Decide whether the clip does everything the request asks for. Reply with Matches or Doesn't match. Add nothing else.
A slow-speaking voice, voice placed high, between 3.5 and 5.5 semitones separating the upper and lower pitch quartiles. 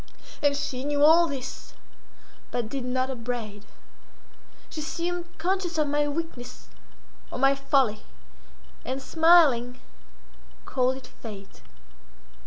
Matches